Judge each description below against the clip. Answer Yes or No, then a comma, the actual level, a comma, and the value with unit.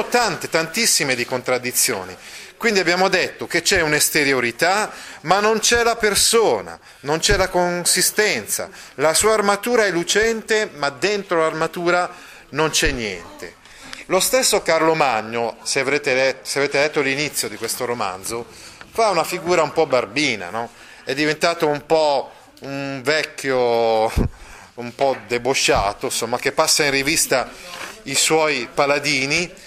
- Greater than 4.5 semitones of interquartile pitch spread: Yes, wide, 5.6 semitones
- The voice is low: No, medium, 155 Hz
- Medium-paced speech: Yes, average, 135 wpm